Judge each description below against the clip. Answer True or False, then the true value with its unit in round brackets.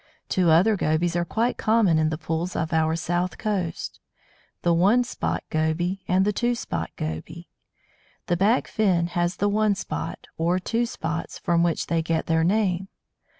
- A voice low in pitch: False (175 Hz)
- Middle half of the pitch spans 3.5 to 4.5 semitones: True (3.8 semitones)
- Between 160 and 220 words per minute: True (170 wpm)